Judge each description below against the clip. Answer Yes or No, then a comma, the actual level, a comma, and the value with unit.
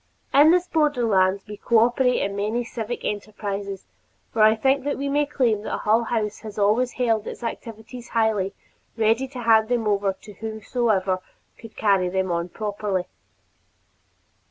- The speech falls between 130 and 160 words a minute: Yes, average, 150 wpm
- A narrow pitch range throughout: No, average, 3.1 semitones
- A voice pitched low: No, high, 220 Hz